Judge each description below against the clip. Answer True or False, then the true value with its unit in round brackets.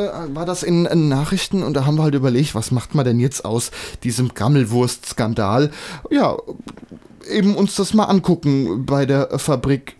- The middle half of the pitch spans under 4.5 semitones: False (5.6 semitones)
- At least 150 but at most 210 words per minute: True (160 wpm)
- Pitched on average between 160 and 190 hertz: False (140 Hz)